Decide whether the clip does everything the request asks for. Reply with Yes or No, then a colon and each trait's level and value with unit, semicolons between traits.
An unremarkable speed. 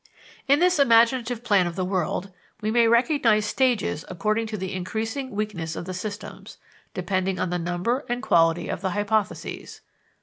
Yes: average, 165 wpm